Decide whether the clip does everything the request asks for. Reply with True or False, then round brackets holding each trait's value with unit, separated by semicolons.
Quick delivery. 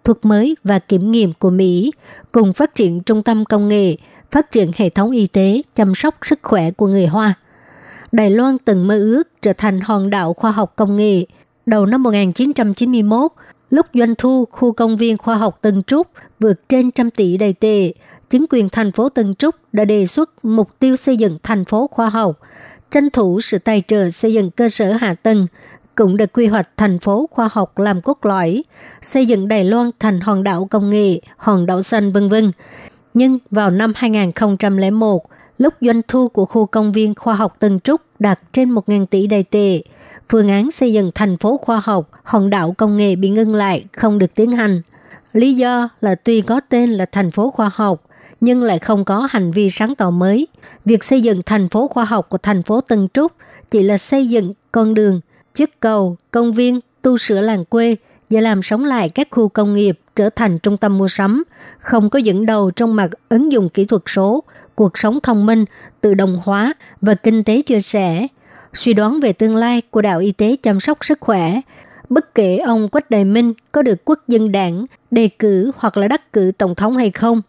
False (210 wpm)